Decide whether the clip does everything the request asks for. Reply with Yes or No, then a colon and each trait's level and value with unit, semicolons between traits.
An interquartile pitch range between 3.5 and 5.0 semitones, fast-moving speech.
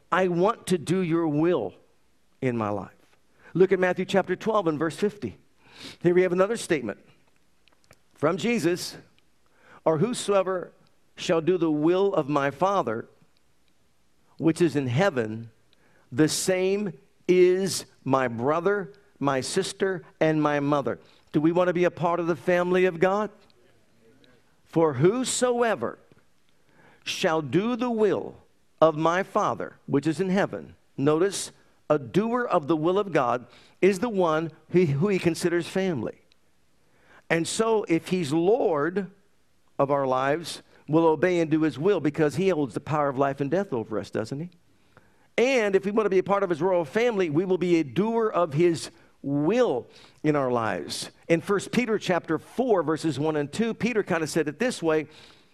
No: average, 4.0 semitones; average, 165 wpm